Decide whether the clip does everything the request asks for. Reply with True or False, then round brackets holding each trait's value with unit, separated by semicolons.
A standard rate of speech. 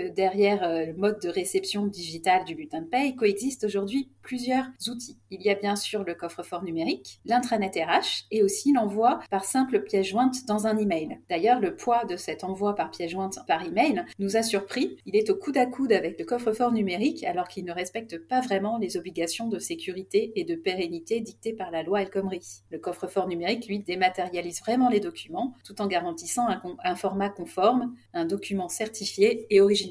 True (195 wpm)